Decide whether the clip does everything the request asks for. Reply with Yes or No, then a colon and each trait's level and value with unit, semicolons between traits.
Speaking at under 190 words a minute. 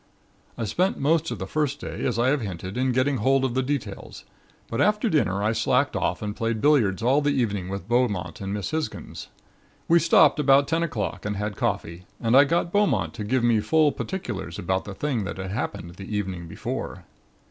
No: average, 200 wpm